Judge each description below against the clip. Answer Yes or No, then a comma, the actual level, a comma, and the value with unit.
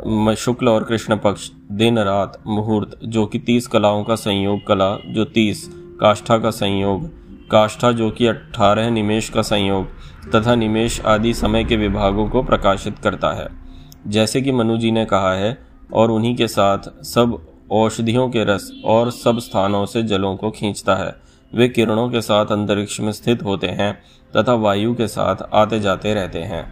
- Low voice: Yes, low, 110 Hz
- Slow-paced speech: No, average, 160 wpm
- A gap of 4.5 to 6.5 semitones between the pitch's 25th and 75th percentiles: No, narrow, 2.4 semitones